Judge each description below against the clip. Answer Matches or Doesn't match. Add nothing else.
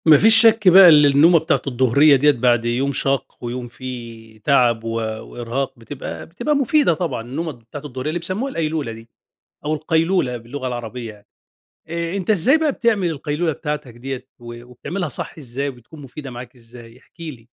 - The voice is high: Doesn't match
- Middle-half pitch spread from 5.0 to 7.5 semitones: Matches